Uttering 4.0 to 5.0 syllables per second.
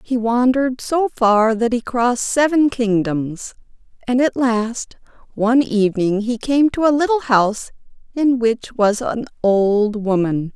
Yes: 4.2 syllables/s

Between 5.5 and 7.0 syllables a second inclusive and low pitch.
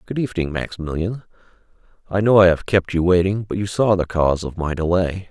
Yes: 6.0 syllables/s; very low, 90 Hz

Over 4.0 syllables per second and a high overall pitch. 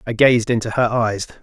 No: 5.2 syllables/s; low, 115 Hz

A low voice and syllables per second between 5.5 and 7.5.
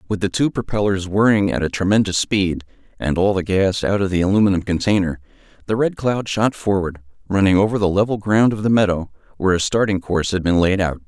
Yes: low, 100 Hz; 6.0 syllables/s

